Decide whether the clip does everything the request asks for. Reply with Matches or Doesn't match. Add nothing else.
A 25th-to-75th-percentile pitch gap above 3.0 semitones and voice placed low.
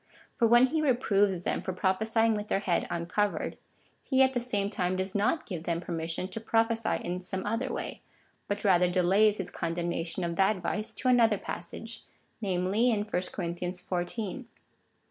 Doesn't match